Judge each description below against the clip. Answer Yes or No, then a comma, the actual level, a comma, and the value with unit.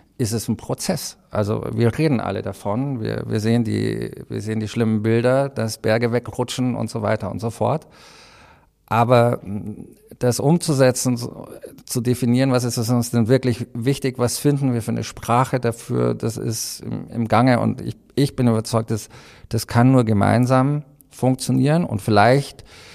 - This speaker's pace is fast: No, average, 165 wpm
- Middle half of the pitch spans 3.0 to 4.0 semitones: No, narrow, 2.6 semitones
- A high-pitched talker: No, low, 120 Hz